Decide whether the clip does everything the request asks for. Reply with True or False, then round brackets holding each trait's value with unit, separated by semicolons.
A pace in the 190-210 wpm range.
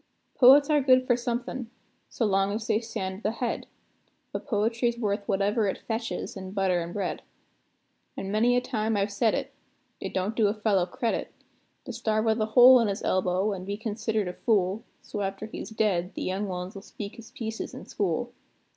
True (200 wpm)